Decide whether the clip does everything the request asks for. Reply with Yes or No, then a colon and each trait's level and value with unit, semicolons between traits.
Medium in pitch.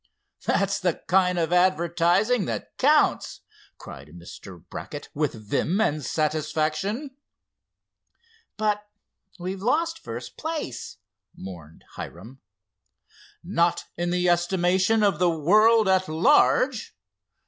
Yes: medium, 180 Hz